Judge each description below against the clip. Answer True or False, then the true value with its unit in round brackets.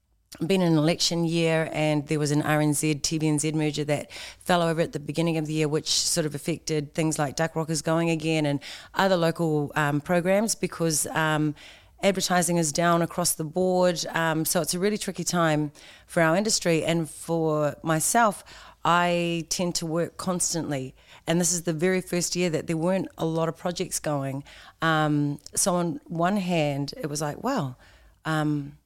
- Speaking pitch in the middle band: True (160 Hz)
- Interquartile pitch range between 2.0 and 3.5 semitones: True (2.4 semitones)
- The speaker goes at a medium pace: True (180 wpm)